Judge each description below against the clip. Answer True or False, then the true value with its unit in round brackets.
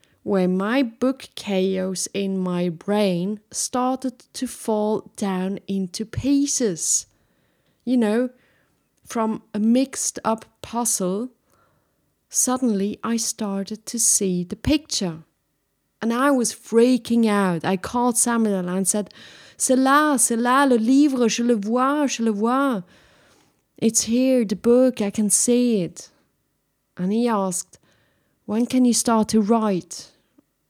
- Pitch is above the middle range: True (225 Hz)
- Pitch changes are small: False (3.9 semitones)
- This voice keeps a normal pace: False (130 wpm)